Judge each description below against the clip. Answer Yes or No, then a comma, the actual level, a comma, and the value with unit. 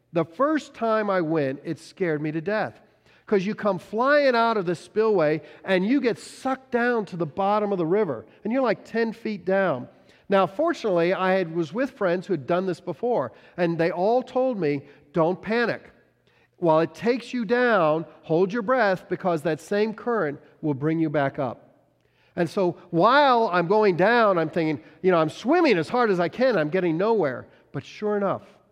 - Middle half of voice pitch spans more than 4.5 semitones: Yes, wide, 5.5 semitones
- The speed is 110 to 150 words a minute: No, average, 195 wpm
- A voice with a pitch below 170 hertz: No, high, 190 Hz